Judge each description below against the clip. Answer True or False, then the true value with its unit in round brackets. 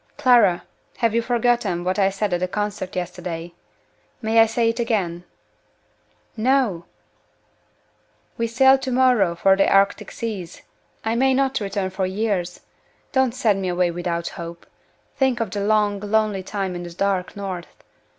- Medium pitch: False (200 Hz)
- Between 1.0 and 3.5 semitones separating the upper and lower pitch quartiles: False (4.2 semitones)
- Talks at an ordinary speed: True (155 wpm)